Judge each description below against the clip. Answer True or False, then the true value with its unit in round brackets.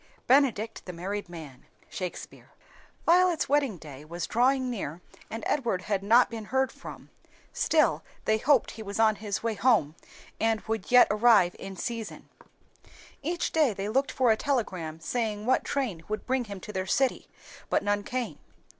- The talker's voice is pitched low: False (220 Hz)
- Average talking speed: True (165 wpm)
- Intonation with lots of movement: False (4.7 semitones)